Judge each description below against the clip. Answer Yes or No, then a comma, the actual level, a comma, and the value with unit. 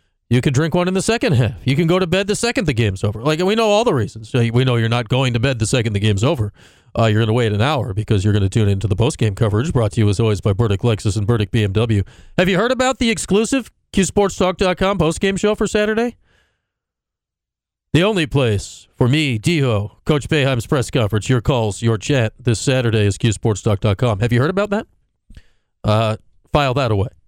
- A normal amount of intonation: No, wide, 6.8 semitones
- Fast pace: Yes, fast, 225 wpm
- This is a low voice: Yes, low, 120 Hz